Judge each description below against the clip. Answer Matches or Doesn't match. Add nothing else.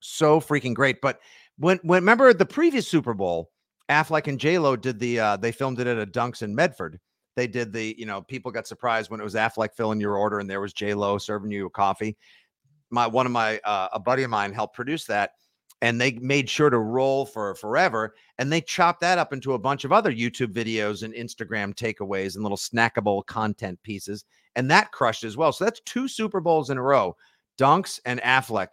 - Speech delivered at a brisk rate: Matches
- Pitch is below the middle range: Matches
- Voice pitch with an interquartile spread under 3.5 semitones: Doesn't match